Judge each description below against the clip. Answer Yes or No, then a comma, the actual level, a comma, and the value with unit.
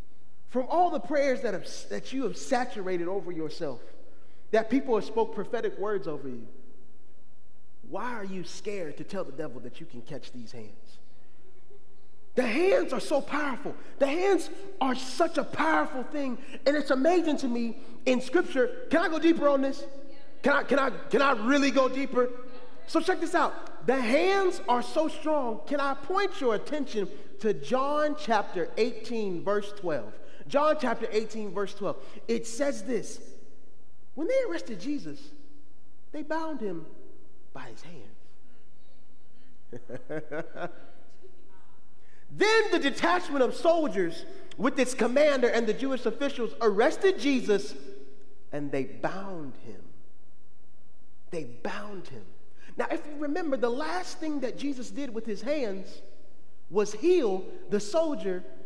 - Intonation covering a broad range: Yes, wide, 6.5 semitones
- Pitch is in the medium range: No, very high, 255 Hz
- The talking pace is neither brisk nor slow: Yes, average, 145 wpm